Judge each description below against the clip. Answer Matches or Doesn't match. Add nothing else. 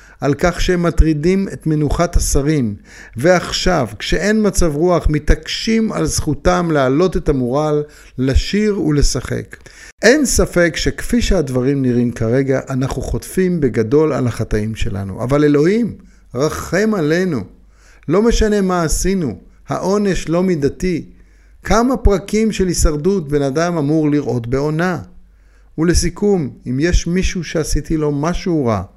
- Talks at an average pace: Matches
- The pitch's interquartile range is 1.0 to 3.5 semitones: Doesn't match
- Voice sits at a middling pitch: Matches